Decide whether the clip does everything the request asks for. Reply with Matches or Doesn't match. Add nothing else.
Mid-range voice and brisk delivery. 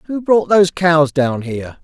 Doesn't match